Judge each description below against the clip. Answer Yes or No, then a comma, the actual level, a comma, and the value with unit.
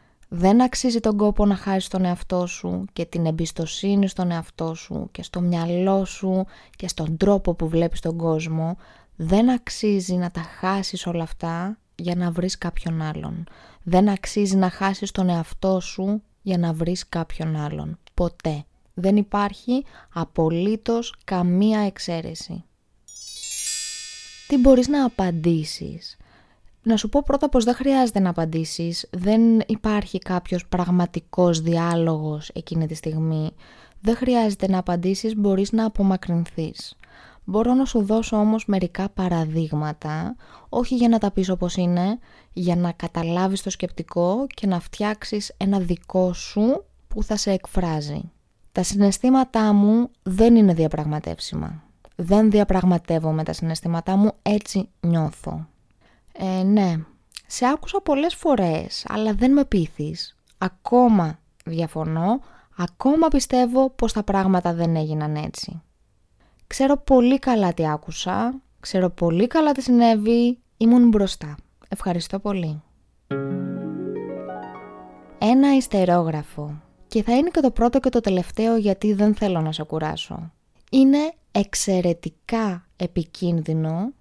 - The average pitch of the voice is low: No, medium, 185 Hz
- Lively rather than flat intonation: No, average, 4.5 semitones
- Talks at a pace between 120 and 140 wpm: Yes, average, 130 wpm